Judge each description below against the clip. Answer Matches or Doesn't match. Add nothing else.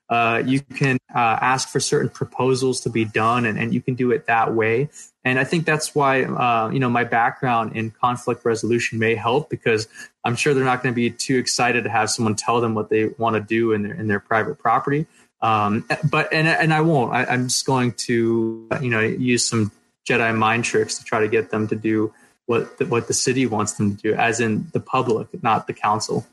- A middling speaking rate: Doesn't match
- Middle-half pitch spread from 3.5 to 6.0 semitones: Doesn't match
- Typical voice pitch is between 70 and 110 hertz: Doesn't match